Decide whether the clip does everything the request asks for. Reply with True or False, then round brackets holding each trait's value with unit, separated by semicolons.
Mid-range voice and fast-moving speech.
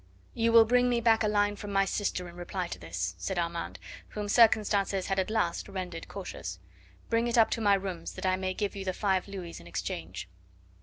False (195 Hz; 215 wpm)